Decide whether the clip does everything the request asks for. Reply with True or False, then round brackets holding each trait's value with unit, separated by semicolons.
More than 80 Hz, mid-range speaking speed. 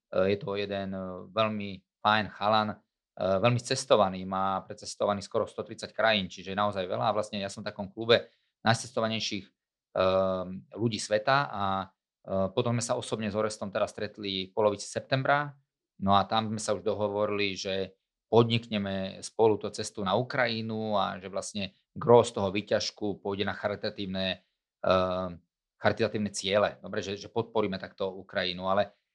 True (105 Hz; 145 wpm)